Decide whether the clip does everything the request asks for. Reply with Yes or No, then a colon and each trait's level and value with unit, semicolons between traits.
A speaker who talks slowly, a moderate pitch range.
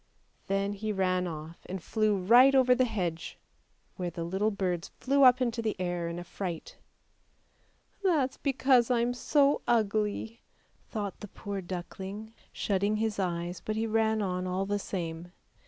No: average, 170 wpm; average, 4.0 semitones